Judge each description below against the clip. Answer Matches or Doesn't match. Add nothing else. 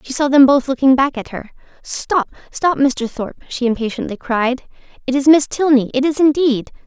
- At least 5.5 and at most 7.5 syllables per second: Doesn't match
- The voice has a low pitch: Doesn't match